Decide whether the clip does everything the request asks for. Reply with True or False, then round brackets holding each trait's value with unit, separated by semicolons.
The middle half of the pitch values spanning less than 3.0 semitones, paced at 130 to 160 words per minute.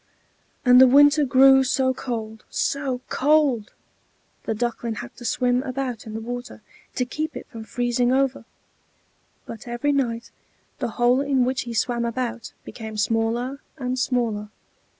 True (2.4 semitones; 150 wpm)